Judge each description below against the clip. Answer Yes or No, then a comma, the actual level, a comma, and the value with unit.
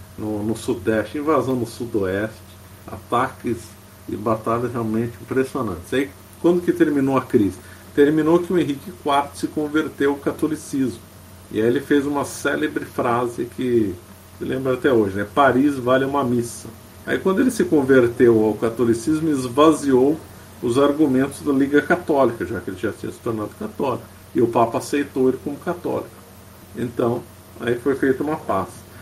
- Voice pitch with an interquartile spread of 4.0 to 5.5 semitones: Yes, average, 4.5 semitones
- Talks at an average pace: Yes, average, 160 wpm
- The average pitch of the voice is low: Yes, low, 125 Hz